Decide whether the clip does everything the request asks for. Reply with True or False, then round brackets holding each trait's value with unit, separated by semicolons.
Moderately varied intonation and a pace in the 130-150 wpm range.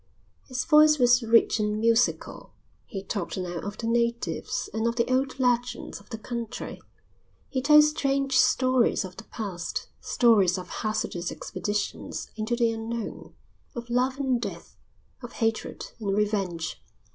True (3.2 semitones; 145 wpm)